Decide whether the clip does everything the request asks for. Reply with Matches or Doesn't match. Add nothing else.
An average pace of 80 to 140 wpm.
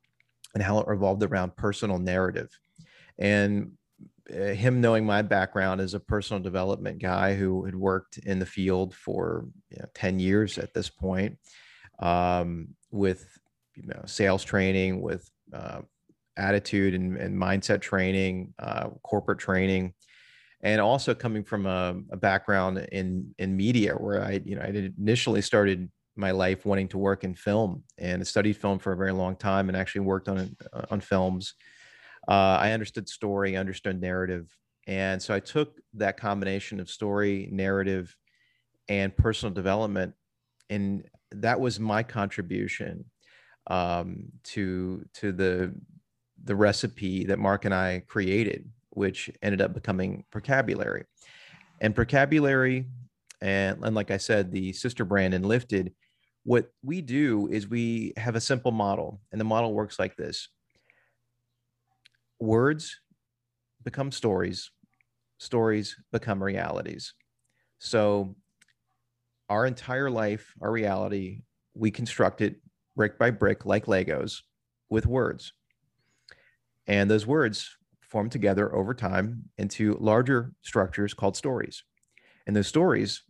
Matches